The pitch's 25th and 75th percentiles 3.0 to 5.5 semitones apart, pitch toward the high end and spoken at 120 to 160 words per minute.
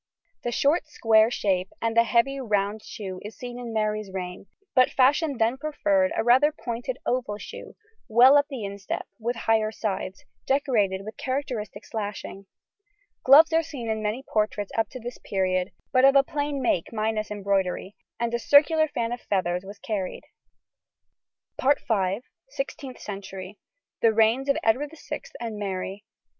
Yes: average, 4.5 semitones; high, 225 Hz; average, 155 wpm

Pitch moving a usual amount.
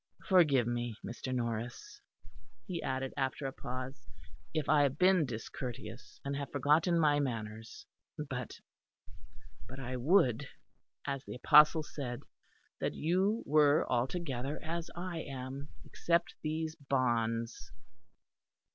Yes: average, 4.1 semitones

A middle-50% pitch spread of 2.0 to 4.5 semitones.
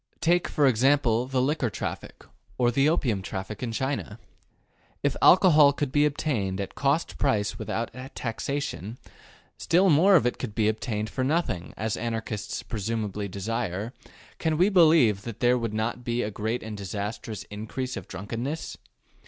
No: average, 5.1 semitones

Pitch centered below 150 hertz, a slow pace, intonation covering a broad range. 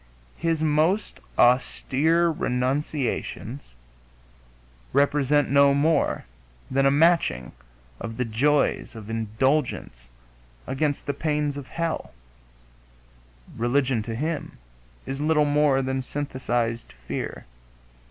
No: medium, 140 Hz; slow, 95 wpm; average, 3.2 semitones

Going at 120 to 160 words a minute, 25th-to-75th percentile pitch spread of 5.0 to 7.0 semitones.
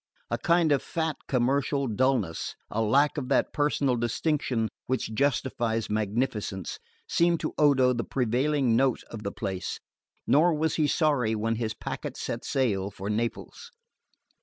No: average, 145 wpm; average, 4.5 semitones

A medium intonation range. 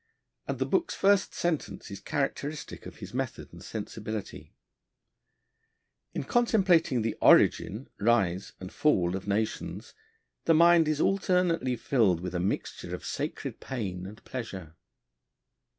No: wide, 9.0 semitones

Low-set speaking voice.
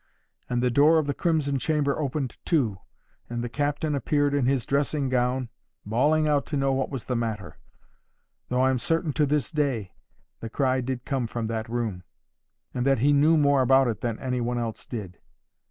Yes: low, 130 Hz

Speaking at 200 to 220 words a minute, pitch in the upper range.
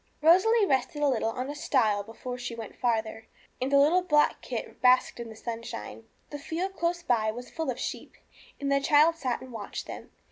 Yes: fast, 205 wpm; very high, 260 Hz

